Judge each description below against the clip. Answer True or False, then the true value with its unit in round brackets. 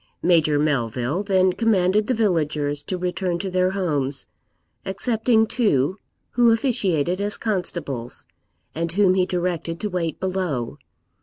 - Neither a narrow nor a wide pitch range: True (4.8 semitones)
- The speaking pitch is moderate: True (180 Hz)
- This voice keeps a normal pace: False (130 wpm)